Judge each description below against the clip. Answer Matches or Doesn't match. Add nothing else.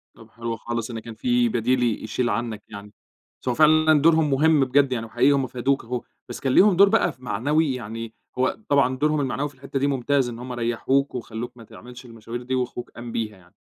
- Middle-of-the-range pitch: Doesn't match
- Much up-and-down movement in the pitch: Doesn't match